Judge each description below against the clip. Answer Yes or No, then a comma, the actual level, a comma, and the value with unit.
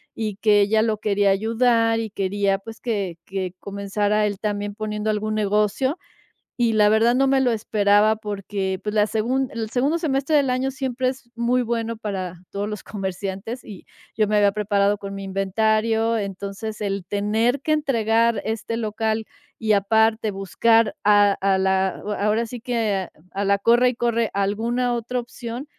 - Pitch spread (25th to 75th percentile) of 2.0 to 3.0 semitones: Yes, narrow, 2.4 semitones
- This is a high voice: Yes, high, 215 Hz